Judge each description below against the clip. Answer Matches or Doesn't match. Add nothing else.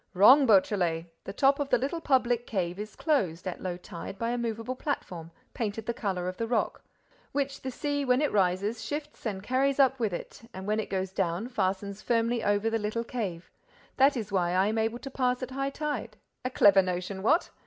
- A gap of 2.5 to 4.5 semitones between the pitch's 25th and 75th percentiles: Doesn't match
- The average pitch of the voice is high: Matches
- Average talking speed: Doesn't match